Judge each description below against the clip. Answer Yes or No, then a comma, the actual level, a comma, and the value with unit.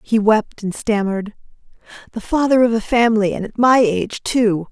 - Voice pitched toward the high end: Yes, high, 220 Hz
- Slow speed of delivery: No, average, 180 wpm